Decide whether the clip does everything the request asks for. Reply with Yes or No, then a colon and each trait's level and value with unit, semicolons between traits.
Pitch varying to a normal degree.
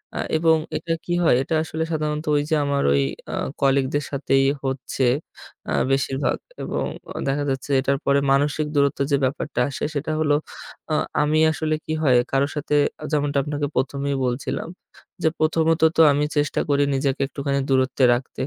No: narrow, 2.0 semitones